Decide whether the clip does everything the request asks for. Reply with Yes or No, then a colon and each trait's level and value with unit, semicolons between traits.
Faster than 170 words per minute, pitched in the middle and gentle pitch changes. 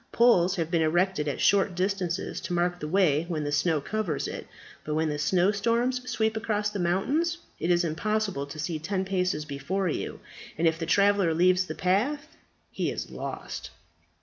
No: average, 180 wpm; medium, 180 Hz; average, 4.0 semitones